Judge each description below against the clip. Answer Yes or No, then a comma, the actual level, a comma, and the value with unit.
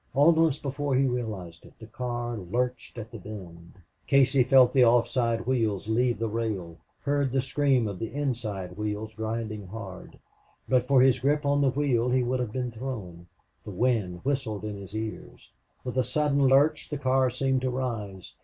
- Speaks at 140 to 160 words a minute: No, average, 180 wpm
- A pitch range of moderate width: Yes, average, 3.7 semitones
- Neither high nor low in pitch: No, low, 120 Hz